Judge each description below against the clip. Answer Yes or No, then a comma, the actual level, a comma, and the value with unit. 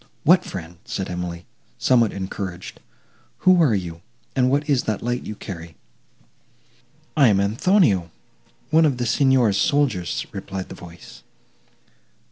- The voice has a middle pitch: No, low, 105 Hz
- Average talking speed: No, slow, 130 wpm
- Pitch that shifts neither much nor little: No, wide, 7.1 semitones